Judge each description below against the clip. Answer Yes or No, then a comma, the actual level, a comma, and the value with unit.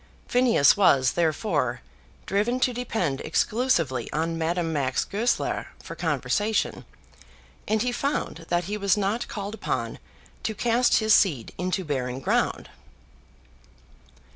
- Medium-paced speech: No, slow, 120 wpm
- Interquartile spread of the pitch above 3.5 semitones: Yes, wide, 5.6 semitones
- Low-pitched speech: No, high, 195 Hz